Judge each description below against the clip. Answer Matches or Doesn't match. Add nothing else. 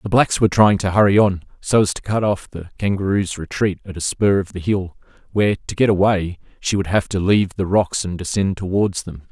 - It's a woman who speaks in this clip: Doesn't match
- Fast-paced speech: Matches